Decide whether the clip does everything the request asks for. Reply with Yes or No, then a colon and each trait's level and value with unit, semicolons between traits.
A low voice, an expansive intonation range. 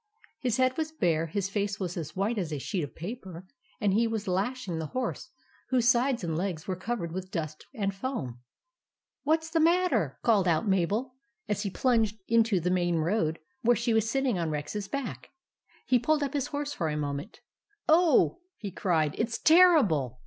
No: high, 205 Hz; wide, 6.9 semitones